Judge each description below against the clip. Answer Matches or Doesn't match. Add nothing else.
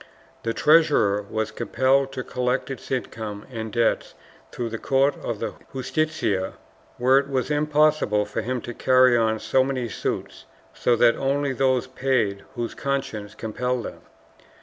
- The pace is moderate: Matches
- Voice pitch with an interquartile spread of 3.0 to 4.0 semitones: Matches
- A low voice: Matches